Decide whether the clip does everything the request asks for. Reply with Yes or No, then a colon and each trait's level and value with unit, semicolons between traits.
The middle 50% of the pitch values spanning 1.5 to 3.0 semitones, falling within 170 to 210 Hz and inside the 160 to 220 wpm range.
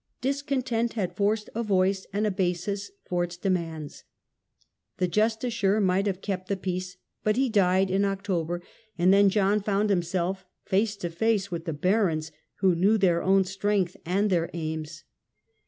Yes: average, 2.7 semitones; high, 190 Hz; average, 165 wpm